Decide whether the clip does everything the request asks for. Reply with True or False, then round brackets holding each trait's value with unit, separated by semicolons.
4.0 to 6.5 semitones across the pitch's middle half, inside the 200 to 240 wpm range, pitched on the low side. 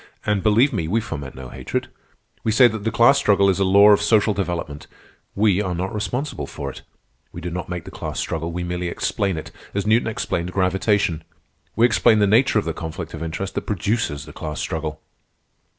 True (4.3 semitones; 205 wpm; 95 Hz)